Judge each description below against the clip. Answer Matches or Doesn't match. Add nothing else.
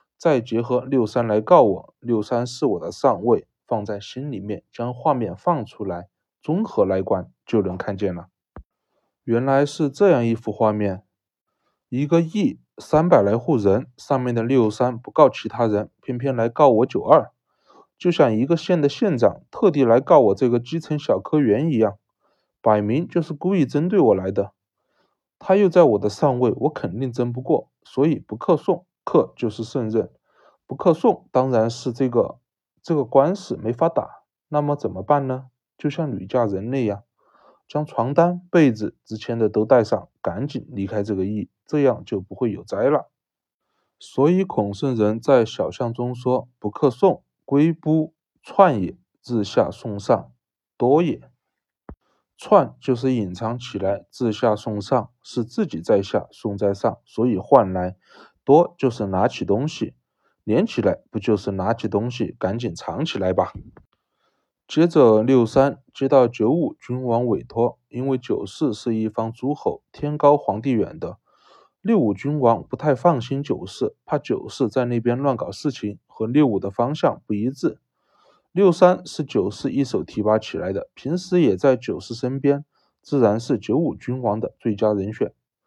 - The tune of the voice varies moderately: Matches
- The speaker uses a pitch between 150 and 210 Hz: Doesn't match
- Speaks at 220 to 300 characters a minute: Matches